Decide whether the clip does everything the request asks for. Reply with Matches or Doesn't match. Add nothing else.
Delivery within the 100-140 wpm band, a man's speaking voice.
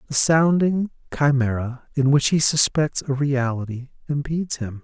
Matches